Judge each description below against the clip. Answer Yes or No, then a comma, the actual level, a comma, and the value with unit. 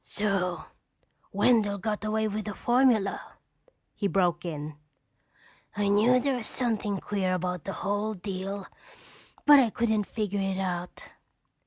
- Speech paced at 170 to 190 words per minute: No, slow, 135 wpm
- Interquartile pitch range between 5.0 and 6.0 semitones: No, narrow, 2.6 semitones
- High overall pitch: Yes, high, 205 Hz